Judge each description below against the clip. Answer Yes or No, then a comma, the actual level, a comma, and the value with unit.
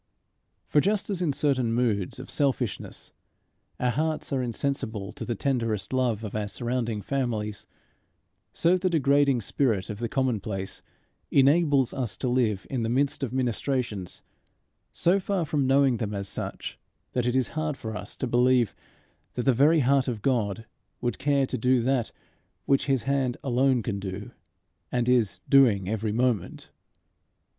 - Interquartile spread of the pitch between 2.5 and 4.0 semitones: Yes, average, 3.7 semitones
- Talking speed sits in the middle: Yes, average, 160 wpm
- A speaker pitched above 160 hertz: No, low, 125 Hz